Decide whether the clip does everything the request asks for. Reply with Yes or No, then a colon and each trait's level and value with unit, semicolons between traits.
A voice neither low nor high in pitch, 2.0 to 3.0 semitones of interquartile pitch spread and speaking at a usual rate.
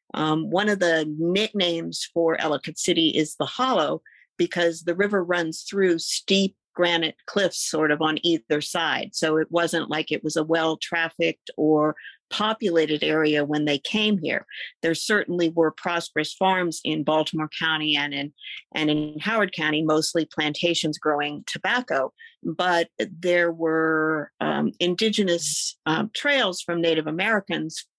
Yes: medium, 165 Hz; narrow, 2.5 semitones; average, 145 wpm